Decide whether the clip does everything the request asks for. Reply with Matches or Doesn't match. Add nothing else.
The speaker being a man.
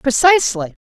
Doesn't match